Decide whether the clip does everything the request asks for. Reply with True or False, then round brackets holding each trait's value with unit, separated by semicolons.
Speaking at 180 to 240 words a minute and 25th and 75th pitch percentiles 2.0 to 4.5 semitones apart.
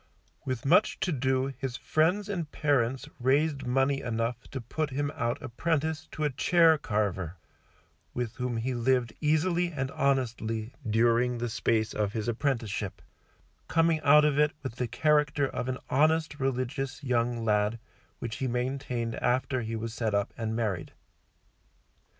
False (150 wpm; 4.0 semitones)